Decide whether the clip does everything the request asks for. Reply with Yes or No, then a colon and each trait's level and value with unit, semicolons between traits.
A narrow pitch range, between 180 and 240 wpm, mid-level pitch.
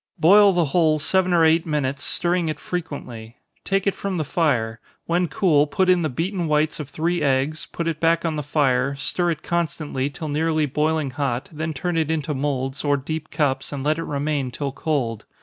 No: average, 3.0 semitones; average, 200 wpm; medium, 155 Hz